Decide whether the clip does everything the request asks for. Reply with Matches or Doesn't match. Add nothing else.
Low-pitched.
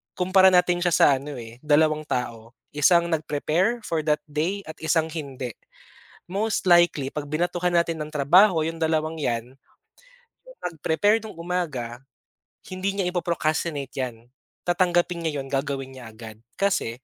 Doesn't match